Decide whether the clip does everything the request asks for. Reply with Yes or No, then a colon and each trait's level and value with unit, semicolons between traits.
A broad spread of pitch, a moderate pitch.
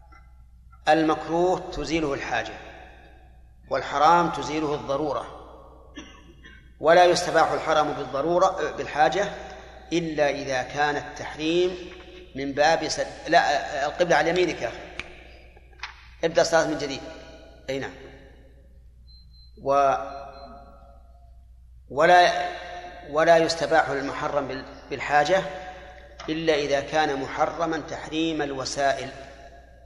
Yes: wide, 6.4 semitones; medium, 145 Hz